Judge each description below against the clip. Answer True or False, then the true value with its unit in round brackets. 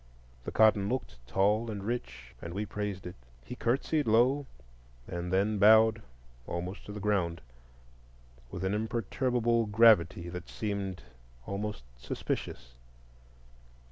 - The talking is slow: True (120 wpm)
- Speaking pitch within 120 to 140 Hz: False (105 Hz)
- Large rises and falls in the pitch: False (3.5 semitones)